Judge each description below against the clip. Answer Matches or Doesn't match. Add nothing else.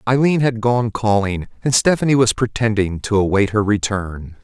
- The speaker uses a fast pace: Doesn't match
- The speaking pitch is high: Doesn't match